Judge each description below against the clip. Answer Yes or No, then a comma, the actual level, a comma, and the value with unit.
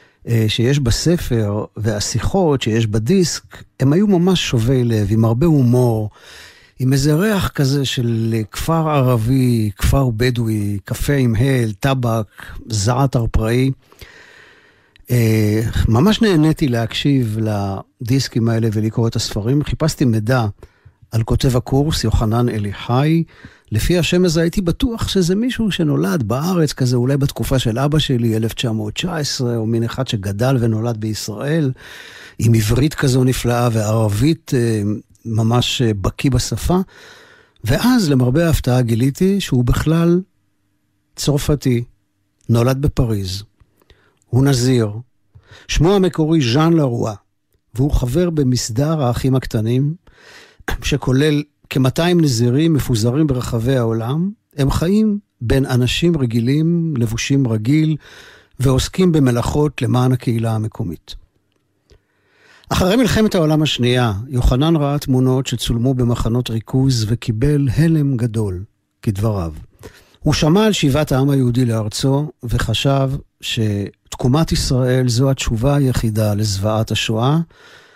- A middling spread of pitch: Yes, average, 4.6 semitones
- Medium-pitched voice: No, low, 125 Hz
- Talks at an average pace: Yes, average, 110 wpm